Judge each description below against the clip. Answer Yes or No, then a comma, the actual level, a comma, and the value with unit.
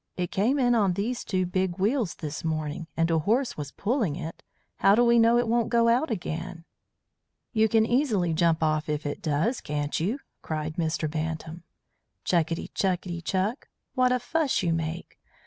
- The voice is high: No, medium, 180 Hz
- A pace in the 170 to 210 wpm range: Yes, average, 180 wpm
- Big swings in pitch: Yes, wide, 6.4 semitones